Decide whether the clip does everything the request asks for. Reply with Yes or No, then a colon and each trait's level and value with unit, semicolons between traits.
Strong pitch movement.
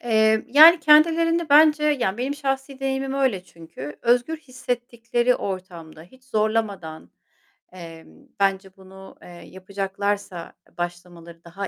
Yes: wide, 6.7 semitones